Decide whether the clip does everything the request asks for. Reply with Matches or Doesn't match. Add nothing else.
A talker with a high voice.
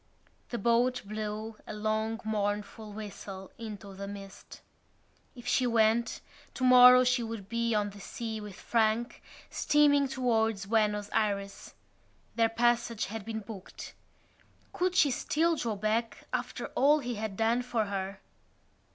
Matches